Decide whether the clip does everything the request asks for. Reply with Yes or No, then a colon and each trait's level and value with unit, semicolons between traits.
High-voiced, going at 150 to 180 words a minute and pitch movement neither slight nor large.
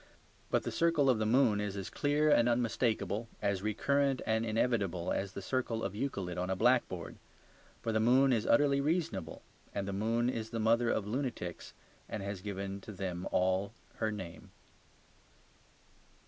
No: low, 110 Hz; average, 165 wpm; average, 4.1 semitones